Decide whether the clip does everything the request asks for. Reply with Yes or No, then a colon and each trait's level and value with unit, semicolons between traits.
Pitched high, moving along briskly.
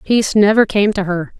Yes: high, 200 Hz; fast, 215 wpm